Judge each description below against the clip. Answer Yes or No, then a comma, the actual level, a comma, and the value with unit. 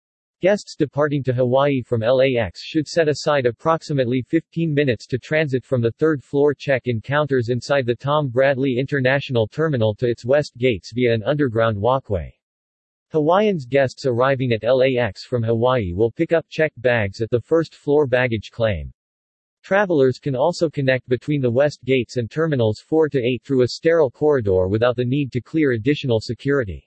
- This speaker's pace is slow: No, average, 170 wpm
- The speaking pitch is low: Yes, low, 130 Hz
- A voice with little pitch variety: No, average, 3.9 semitones